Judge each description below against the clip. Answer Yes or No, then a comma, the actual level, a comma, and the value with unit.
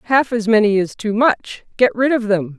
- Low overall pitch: No, high, 220 Hz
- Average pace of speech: No, fast, 230 wpm